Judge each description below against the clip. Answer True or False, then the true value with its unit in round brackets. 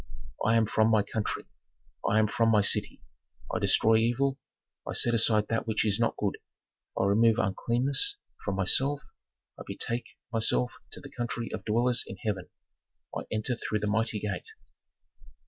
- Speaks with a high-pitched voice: False (110 Hz)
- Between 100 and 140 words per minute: False (165 wpm)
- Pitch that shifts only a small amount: True (2.0 semitones)